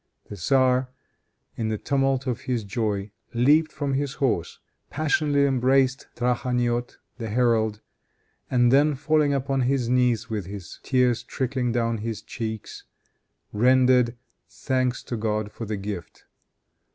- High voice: No, low, 125 Hz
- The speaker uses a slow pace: Yes, slow, 125 wpm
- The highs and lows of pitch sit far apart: No, average, 3.0 semitones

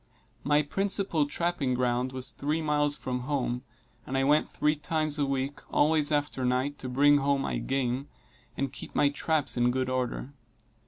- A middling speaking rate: Yes, average, 170 wpm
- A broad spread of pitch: No, narrow, 2.6 semitones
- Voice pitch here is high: No, medium, 140 Hz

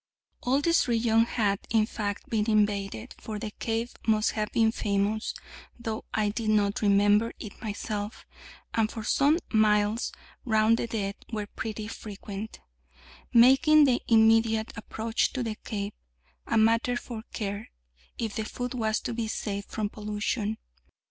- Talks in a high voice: Yes, high, 220 Hz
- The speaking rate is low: No, average, 150 wpm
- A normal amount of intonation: No, narrow, 1.6 semitones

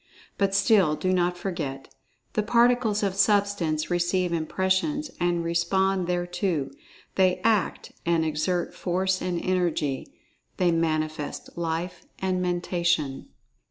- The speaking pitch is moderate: Yes, medium, 180 Hz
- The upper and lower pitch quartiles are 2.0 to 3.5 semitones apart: Yes, narrow, 2.4 semitones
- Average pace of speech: No, slow, 100 wpm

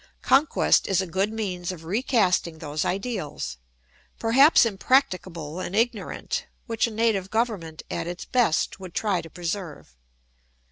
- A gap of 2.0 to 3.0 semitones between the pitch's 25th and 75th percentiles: No, average, 4.9 semitones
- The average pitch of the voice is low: No, high, 190 Hz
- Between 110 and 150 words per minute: Yes, slow, 135 wpm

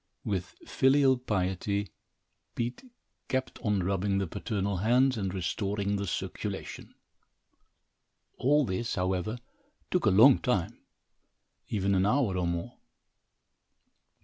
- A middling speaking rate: No, slow, 110 wpm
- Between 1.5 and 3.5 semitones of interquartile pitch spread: No, average, 4.6 semitones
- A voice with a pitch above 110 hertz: No, low, 100 Hz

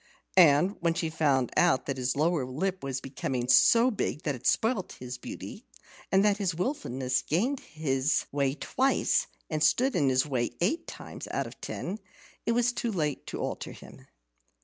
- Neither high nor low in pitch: Yes, medium, 155 Hz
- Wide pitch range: Yes, wide, 6.8 semitones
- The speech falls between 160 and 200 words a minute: Yes, average, 175 wpm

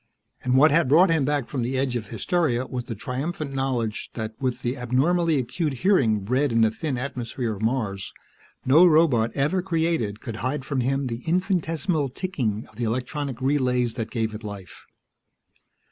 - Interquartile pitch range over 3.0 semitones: Yes, average, 4.5 semitones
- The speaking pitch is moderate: No, low, 130 Hz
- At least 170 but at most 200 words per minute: Yes, average, 175 wpm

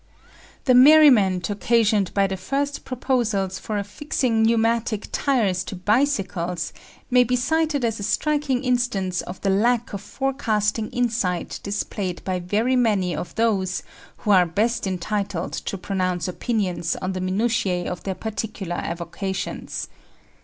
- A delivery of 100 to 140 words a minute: Yes, slow, 135 wpm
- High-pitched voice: Yes, high, 210 Hz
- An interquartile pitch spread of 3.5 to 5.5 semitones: Yes, average, 4.5 semitones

